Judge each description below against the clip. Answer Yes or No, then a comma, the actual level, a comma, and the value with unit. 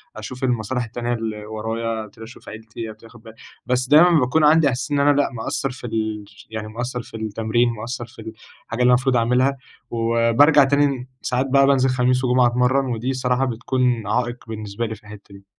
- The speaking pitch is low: Yes, low, 120 Hz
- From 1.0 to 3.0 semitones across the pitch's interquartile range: Yes, narrow, 2.5 semitones